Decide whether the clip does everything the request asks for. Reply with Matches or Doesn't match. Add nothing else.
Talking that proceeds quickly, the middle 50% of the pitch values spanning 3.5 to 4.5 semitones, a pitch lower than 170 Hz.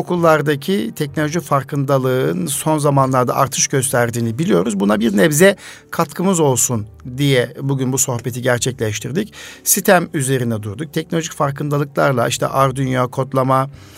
Doesn't match